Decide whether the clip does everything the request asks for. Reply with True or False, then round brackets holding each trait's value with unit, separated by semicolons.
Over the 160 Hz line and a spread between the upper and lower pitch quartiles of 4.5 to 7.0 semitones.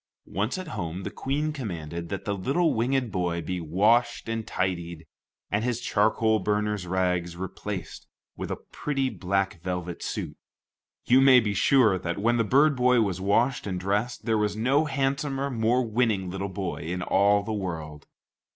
False (105 Hz; 5.2 semitones)